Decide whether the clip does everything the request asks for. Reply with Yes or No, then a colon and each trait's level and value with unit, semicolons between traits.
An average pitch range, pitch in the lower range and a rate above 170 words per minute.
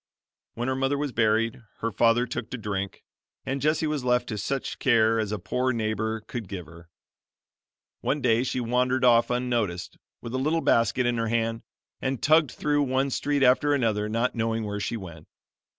Yes: average, 3.0 semitones; low, 120 Hz; average, 185 wpm